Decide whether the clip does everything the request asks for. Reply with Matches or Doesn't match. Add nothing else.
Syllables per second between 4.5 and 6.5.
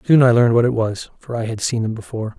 Doesn't match